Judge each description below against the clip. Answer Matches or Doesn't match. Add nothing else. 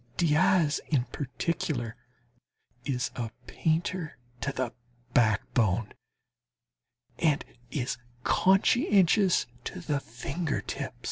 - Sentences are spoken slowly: Matches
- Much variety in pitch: Matches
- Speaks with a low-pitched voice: Doesn't match